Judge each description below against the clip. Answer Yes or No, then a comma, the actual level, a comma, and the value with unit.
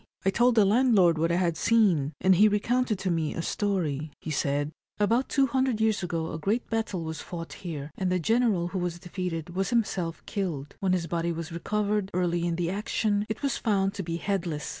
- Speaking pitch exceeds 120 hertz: Yes, medium, 185 Hz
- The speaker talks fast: Yes, fast, 210 wpm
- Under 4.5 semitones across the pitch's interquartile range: Yes, average, 4.1 semitones